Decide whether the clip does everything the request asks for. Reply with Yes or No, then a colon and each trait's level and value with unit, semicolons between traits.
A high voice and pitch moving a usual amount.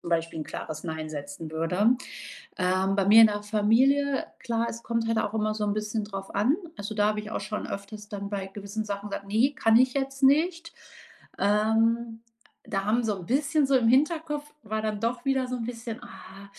Yes: high, 215 Hz; average, 3.5 semitones